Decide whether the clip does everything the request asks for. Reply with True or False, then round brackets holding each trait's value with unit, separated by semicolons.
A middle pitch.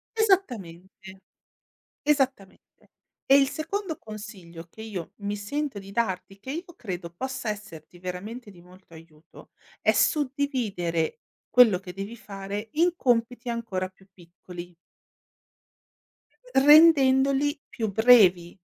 False (210 Hz)